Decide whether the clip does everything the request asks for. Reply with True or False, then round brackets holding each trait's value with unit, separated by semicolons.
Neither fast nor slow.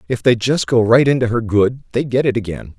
False (260 wpm)